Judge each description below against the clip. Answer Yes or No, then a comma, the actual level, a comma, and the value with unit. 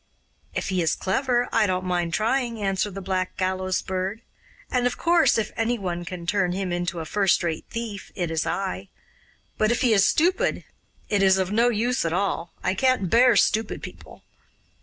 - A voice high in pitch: Yes, high, 195 Hz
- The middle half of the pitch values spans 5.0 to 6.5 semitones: No, average, 4.2 semitones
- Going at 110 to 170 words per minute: No, average, 190 wpm